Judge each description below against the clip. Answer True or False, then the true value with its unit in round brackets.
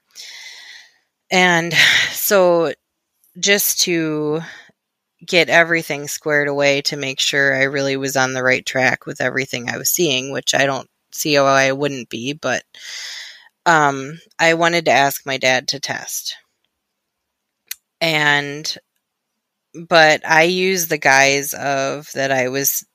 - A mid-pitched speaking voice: True (150 Hz)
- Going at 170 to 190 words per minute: False (135 wpm)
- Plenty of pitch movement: False (3.6 semitones)